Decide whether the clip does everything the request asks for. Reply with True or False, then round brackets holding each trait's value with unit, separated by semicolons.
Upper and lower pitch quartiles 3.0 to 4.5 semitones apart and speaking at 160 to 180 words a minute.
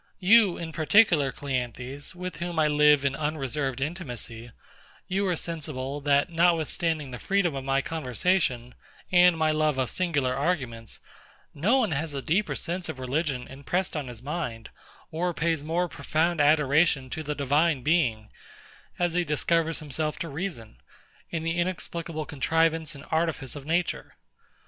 False (3.8 semitones; 150 wpm)